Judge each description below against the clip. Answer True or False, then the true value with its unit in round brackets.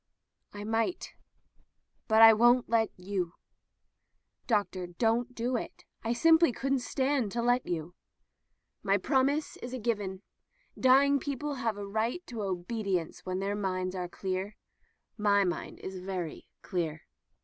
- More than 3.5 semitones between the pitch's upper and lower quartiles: True (4.7 semitones)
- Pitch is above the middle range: True (220 Hz)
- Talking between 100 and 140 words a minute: True (135 wpm)